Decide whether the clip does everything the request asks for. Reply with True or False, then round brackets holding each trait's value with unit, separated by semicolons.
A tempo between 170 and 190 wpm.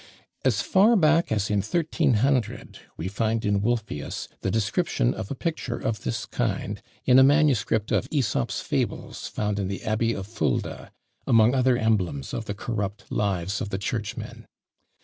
False (160 wpm)